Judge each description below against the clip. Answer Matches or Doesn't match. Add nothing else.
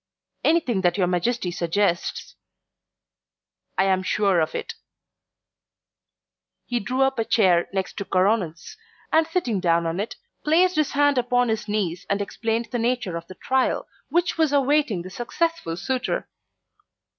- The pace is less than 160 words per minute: Matches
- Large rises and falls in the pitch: Matches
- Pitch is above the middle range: Matches